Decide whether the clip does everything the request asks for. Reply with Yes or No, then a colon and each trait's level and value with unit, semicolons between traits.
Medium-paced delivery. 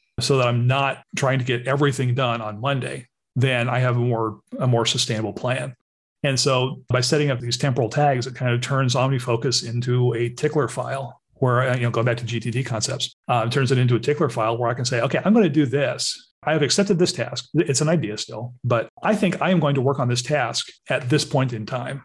No: fast, 240 wpm